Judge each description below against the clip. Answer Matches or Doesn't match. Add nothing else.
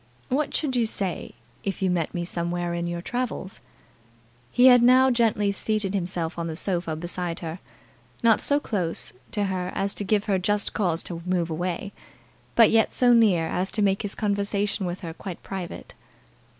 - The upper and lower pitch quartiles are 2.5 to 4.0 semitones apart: Matches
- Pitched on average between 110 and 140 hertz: Doesn't match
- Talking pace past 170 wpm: Matches